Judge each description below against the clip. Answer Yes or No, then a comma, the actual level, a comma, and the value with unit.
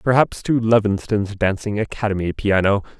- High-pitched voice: No, low, 105 Hz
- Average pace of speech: No, slow, 120 wpm